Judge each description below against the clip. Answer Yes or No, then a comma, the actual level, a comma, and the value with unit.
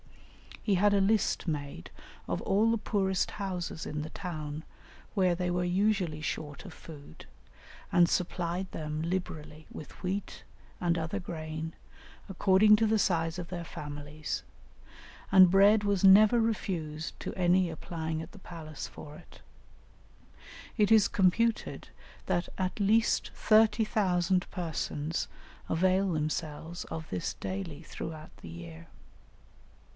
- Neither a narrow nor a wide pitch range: Yes, average, 3.8 semitones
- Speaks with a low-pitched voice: No, medium, 175 Hz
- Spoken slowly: Yes, slow, 130 wpm